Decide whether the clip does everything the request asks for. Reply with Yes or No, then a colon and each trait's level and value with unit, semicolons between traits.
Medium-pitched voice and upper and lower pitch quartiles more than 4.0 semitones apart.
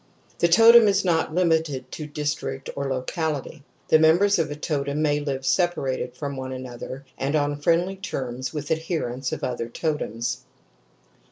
No: medium, 145 Hz; average, 3.7 semitones